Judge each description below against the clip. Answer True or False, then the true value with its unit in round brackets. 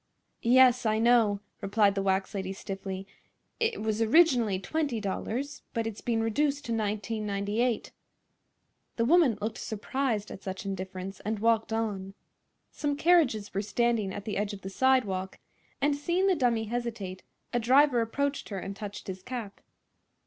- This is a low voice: False (220 Hz)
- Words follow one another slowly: False (150 wpm)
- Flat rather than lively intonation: False (3.9 semitones)